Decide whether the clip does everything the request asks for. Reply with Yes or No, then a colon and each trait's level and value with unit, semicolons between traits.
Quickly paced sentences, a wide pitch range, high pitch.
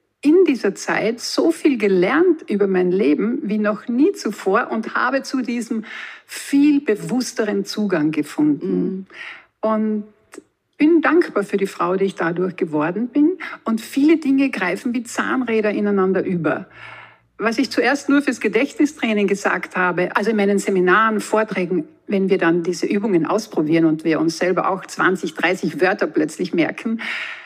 No: average, 150 wpm; wide, 6.6 semitones; high, 220 Hz